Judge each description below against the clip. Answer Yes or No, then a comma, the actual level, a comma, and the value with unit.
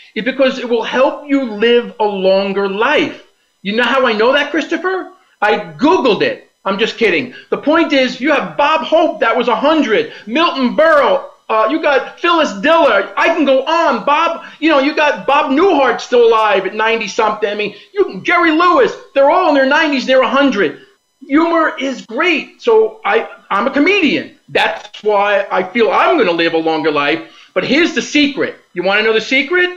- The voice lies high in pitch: Yes, very high, 280 Hz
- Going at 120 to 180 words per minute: No, average, 195 wpm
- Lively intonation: Yes, wide, 6.4 semitones